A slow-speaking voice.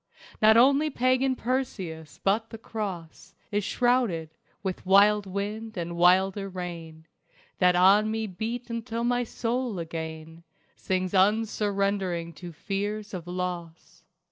Yes: slow, 120 wpm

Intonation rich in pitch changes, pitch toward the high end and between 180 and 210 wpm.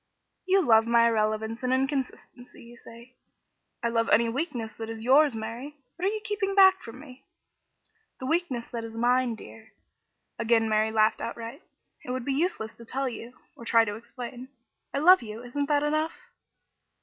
No: average, 3.8 semitones; high, 240 Hz; average, 185 wpm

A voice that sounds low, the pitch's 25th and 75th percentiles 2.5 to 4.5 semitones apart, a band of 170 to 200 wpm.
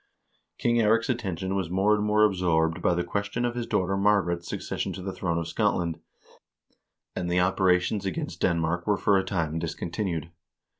Yes: very low, 95 Hz; average, 3.1 semitones; average, 180 wpm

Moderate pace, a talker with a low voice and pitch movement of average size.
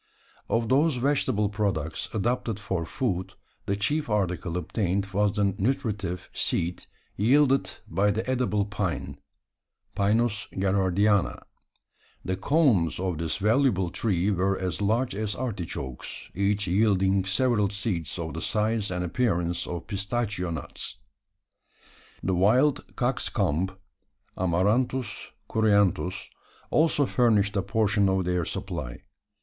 No: slow, 115 wpm; low, 100 Hz; average, 3.5 semitones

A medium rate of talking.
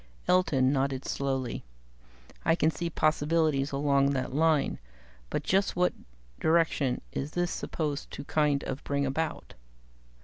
No: slow, 130 wpm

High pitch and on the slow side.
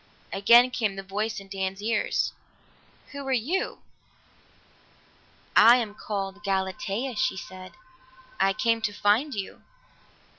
Yes: high, 210 Hz; slow, 120 wpm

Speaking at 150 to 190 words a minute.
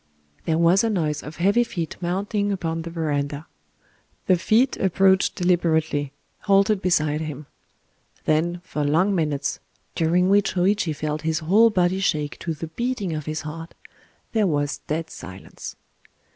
No: slow, 135 wpm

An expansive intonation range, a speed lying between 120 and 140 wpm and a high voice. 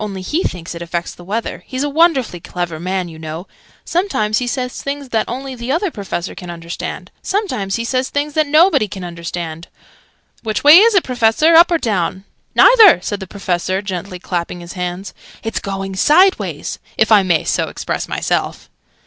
No: wide, 8.2 semitones; average, 185 wpm; high, 210 Hz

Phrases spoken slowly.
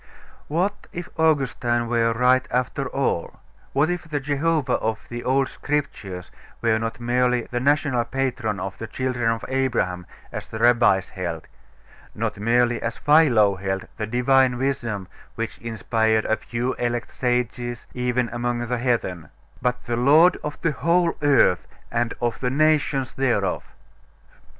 No: average, 145 wpm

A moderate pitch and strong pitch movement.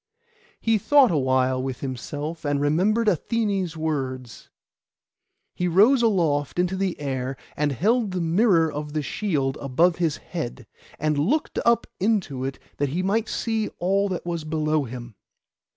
Yes: medium, 160 Hz; wide, 5.8 semitones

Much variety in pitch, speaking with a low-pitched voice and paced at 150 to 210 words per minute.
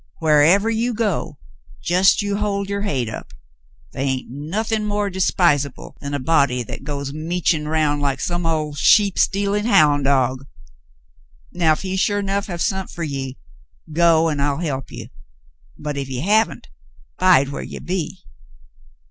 No: wide, 5.8 semitones; medium, 160 Hz; average, 155 wpm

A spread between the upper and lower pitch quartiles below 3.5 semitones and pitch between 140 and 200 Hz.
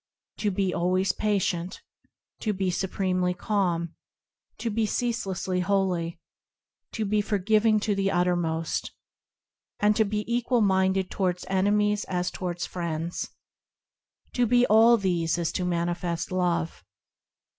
Yes: average, 2.9 semitones; high, 190 Hz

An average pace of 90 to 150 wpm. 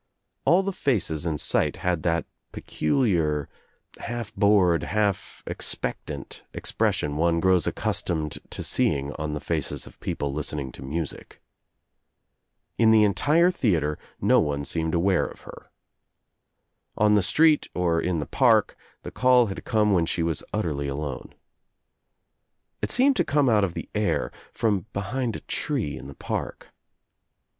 Yes: average, 145 wpm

